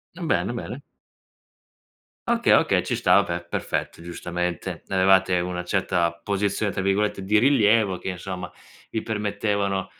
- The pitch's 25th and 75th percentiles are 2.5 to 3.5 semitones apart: Yes, average, 2.9 semitones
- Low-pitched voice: Yes, very low, 95 Hz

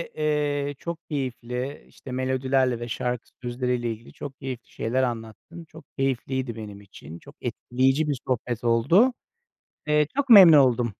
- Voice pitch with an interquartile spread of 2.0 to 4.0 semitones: Yes, average, 3.5 semitones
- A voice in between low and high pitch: No, low, 130 Hz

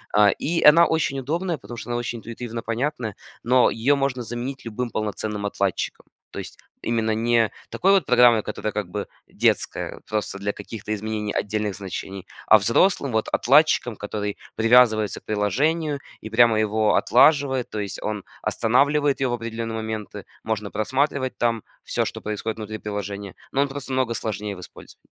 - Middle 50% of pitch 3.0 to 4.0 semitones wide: Yes, average, 3.6 semitones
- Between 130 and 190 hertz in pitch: No, low, 115 Hz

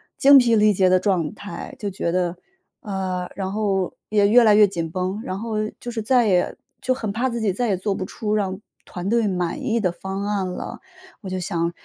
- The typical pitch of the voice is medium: No, high, 200 Hz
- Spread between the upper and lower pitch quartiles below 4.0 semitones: Yes, average, 2.9 semitones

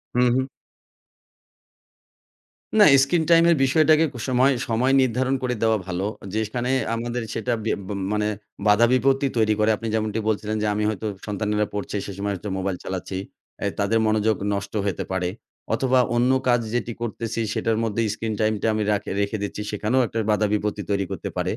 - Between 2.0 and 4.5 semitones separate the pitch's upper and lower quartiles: Yes, average, 3.1 semitones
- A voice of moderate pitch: No, low, 110 Hz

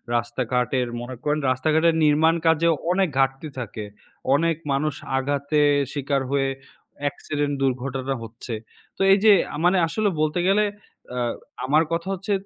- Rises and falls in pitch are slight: No, average, 3.8 semitones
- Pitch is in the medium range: Yes, medium, 145 Hz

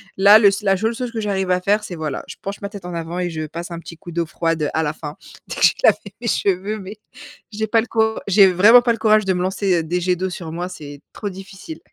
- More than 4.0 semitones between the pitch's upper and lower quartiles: No, average, 3.6 semitones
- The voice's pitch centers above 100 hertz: Yes, high, 190 Hz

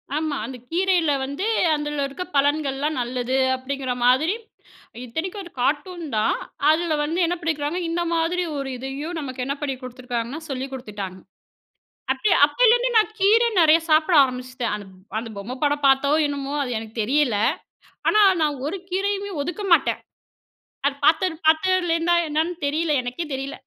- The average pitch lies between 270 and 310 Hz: Yes, very high, 295 Hz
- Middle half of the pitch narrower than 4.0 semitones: No, average, 4.6 semitones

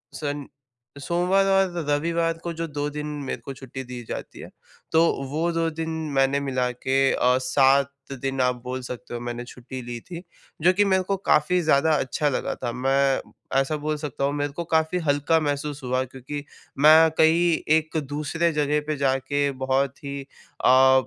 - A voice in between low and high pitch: Yes, medium, 145 Hz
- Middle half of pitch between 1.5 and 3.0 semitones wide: No, average, 3.4 semitones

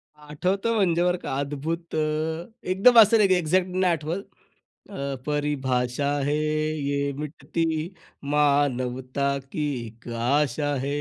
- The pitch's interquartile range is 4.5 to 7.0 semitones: No, average, 3.6 semitones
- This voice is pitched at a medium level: Yes, medium, 150 Hz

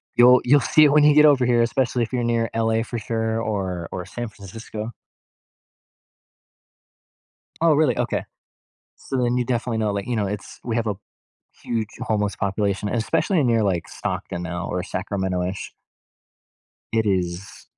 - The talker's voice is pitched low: Yes, low, 115 Hz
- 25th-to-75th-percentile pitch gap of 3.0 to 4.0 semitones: Yes, average, 3.6 semitones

